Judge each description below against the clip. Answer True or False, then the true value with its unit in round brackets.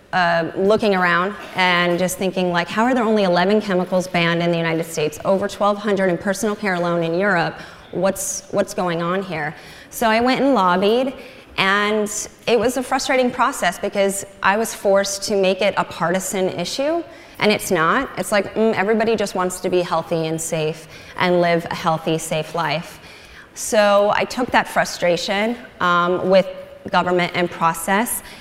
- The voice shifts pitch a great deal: False (3.3 semitones)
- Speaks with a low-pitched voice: False (190 Hz)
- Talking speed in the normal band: True (175 wpm)